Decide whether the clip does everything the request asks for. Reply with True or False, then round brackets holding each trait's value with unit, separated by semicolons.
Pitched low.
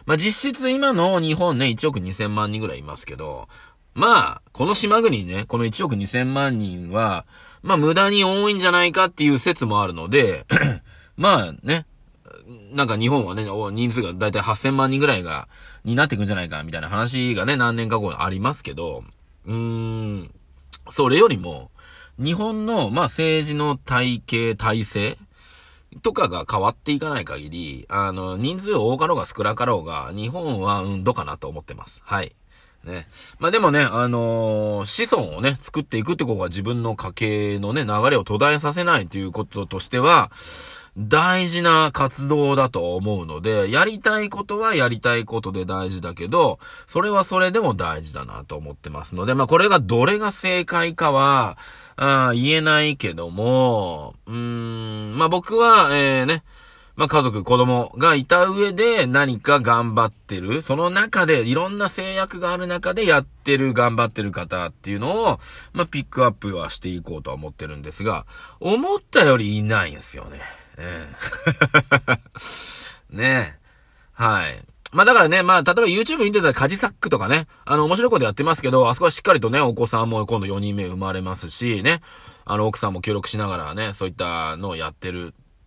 True (120 Hz)